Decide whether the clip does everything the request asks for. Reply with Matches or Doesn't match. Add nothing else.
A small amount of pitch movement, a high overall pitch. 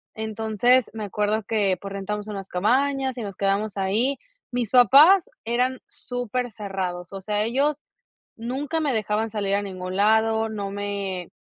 Doesn't match